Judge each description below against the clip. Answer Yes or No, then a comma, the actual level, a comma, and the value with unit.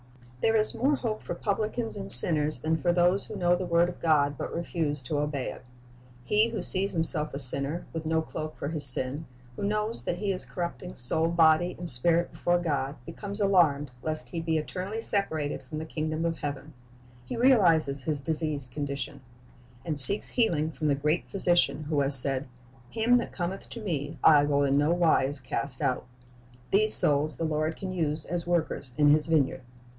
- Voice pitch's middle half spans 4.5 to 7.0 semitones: No, average, 3.7 semitones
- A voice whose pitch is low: No, medium, 160 Hz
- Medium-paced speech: Yes, average, 190 wpm